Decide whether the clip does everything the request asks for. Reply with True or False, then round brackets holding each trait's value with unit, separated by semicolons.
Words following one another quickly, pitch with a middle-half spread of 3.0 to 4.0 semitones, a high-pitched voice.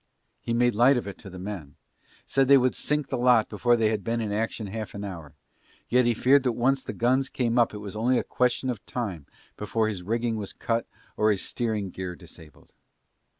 False (220 wpm; 3.4 semitones; 115 Hz)